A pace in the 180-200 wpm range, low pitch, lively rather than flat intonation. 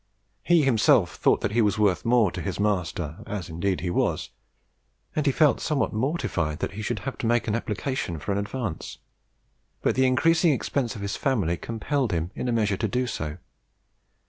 Yes: average, 195 wpm; low, 110 Hz; wide, 5.7 semitones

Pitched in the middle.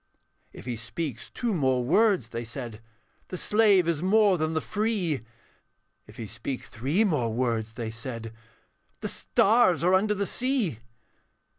Yes: medium, 155 Hz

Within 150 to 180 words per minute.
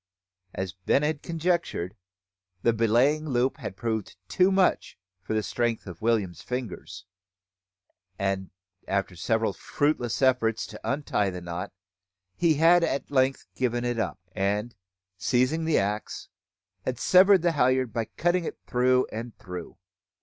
No: average, 140 wpm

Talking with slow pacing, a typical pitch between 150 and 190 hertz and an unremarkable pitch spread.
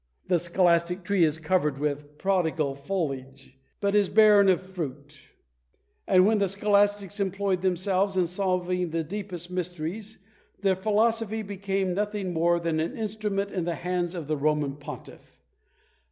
No: average, 145 wpm; medium, 185 Hz; average, 3.5 semitones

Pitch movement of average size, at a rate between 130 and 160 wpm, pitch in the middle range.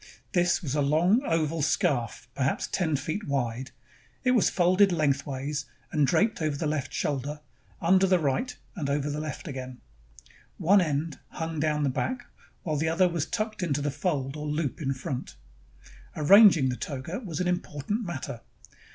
No: average, 4.1 semitones; average, 175 wpm; medium, 150 Hz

